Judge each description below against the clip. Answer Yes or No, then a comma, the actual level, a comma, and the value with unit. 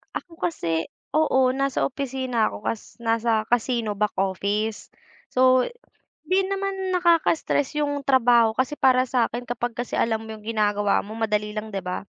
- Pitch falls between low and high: No, high, 240 Hz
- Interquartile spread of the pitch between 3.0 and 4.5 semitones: Yes, average, 4.1 semitones